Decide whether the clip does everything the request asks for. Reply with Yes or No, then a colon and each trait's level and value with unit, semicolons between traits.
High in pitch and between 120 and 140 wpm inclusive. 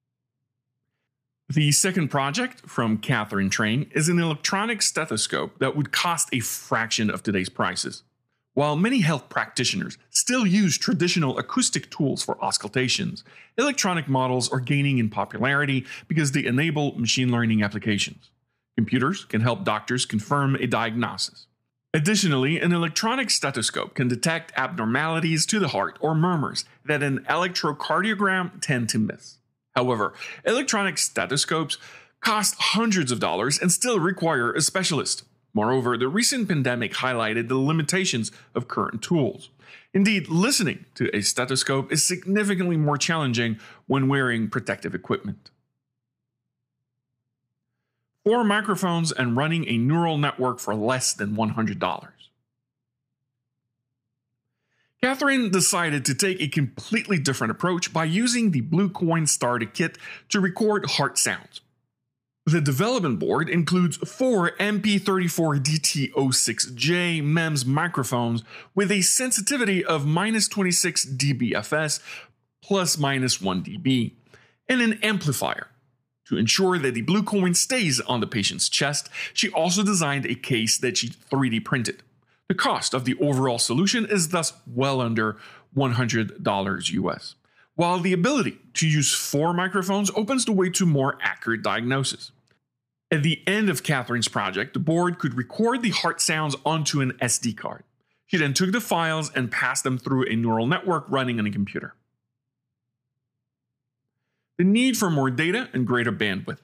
No: medium, 140 Hz; slow, 135 wpm